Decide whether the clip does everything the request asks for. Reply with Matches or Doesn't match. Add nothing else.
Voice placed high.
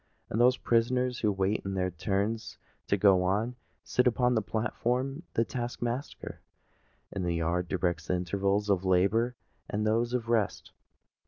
Doesn't match